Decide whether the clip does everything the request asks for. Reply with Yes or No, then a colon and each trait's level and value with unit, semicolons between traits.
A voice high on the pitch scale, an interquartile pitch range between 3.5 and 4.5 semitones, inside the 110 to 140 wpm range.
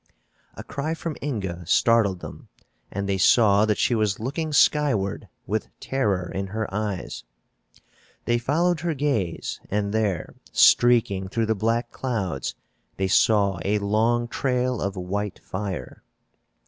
No: low, 110 Hz; average, 4.0 semitones; slow, 135 wpm